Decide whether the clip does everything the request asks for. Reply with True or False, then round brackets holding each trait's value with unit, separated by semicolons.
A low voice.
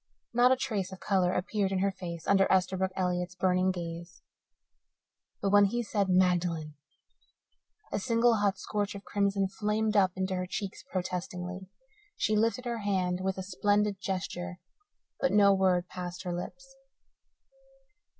False (190 Hz)